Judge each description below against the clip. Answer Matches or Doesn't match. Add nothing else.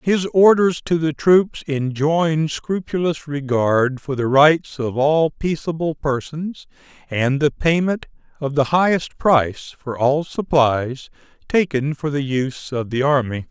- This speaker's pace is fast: Doesn't match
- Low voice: Doesn't match